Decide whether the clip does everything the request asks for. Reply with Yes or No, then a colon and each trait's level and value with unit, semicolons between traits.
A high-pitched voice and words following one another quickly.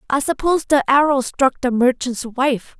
No: very high, 265 Hz; average, 170 wpm